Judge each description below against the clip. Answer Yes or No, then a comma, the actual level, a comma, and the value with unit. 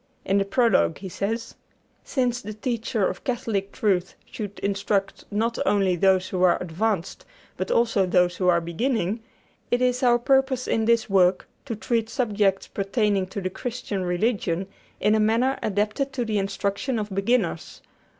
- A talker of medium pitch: No, high, 210 Hz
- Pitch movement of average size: Yes, average, 3.5 semitones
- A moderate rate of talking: Yes, average, 160 wpm